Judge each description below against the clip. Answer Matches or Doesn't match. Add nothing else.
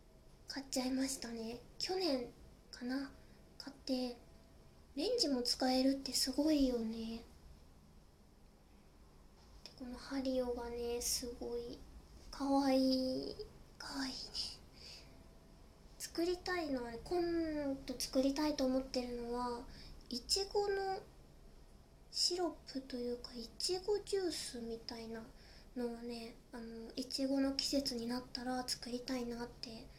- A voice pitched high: Matches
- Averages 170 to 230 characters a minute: Matches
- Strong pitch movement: Doesn't match